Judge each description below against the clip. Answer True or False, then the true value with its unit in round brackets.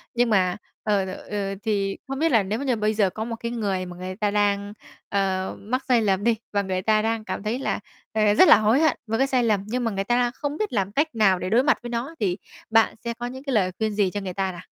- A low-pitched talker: False (215 Hz)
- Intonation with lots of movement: False (3.5 semitones)